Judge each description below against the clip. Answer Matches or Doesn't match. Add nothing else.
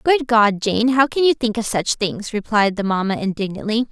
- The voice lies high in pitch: Matches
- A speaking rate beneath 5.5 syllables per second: Matches